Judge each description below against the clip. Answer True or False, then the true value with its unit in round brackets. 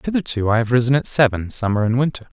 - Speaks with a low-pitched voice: True (125 Hz)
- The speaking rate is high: True (225 wpm)